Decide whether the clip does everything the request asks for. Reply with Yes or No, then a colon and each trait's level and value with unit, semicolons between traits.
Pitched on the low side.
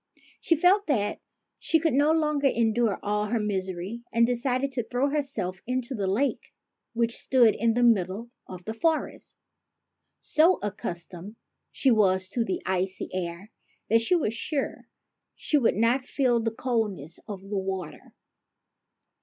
No: high, 230 Hz